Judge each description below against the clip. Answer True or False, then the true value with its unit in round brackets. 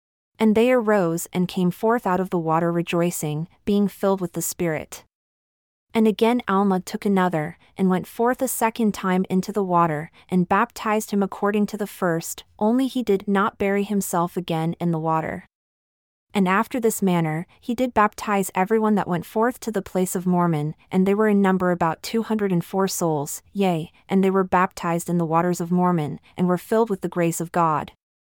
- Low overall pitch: False (190 Hz)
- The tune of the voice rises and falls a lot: False (3.5 semitones)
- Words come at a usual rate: True (195 wpm)